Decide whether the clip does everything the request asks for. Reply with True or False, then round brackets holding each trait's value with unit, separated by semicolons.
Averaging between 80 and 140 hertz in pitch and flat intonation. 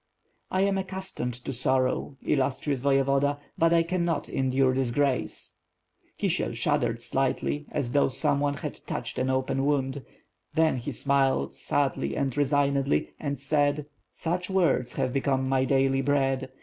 True (135 Hz; 1.7 semitones)